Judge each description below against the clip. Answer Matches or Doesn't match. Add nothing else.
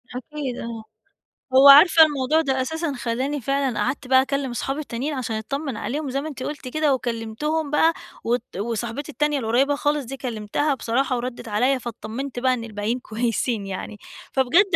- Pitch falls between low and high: Doesn't match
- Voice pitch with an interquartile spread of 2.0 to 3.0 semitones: Doesn't match